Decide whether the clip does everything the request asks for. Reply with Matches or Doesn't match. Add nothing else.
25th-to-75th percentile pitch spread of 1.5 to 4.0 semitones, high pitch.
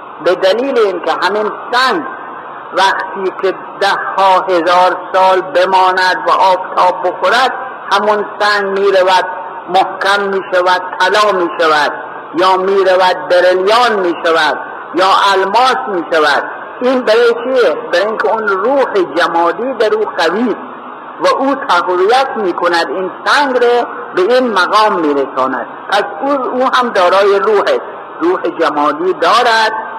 Doesn't match